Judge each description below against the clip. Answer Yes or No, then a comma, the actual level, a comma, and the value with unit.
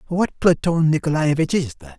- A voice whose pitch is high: No, medium, 155 Hz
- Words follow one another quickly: No, average, 150 wpm